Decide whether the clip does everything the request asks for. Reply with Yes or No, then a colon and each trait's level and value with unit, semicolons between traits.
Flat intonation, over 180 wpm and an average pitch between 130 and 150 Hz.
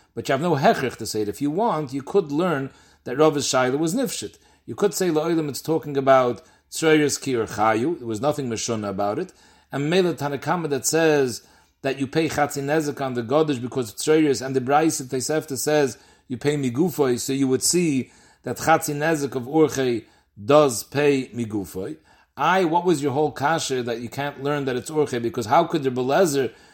No: average, 3.3 semitones; average, 195 wpm; medium, 140 Hz